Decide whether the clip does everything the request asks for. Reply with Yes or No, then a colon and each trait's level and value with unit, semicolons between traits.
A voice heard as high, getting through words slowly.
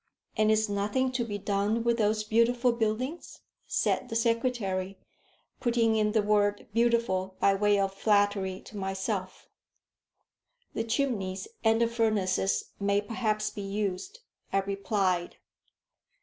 Yes: high, 210 Hz; slow, 130 wpm